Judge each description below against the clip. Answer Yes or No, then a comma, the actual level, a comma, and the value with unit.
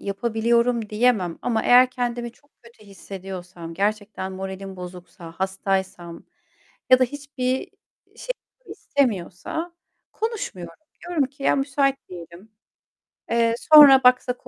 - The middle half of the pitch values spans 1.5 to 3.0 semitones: No, average, 5.2 semitones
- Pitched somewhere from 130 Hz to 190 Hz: No, high, 225 Hz